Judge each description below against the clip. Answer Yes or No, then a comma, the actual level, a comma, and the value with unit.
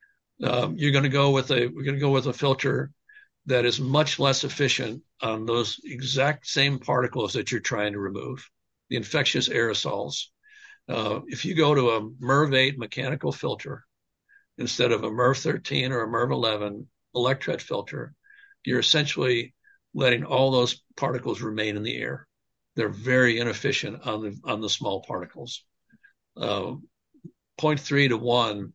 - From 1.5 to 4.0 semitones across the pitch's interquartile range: Yes, average, 3.4 semitones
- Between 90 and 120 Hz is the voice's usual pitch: No, low, 130 Hz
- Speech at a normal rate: Yes, average, 160 wpm